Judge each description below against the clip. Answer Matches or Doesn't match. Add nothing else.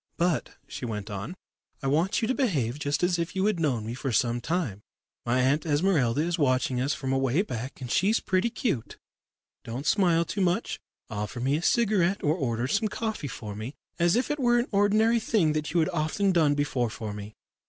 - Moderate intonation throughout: Doesn't match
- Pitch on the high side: Doesn't match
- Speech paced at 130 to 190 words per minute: Doesn't match